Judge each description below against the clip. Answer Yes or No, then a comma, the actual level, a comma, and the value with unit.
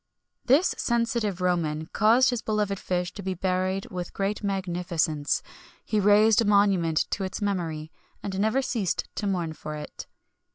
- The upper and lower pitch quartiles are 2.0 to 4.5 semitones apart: Yes, average, 3.2 semitones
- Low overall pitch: No, high, 195 Hz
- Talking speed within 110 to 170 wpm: Yes, average, 155 wpm